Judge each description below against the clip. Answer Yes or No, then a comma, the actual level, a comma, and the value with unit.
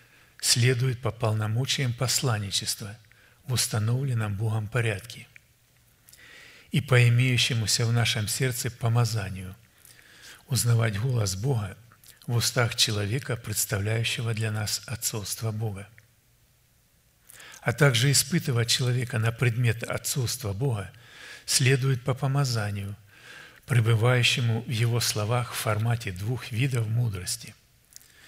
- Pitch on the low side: Yes, low, 120 Hz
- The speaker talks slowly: Yes, slow, 100 wpm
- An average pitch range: No, narrow, 2.2 semitones